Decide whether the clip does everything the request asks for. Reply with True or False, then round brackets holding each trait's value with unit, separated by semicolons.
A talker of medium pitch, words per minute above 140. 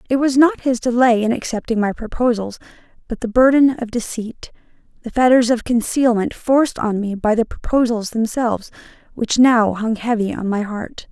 False (235 Hz; 175 wpm)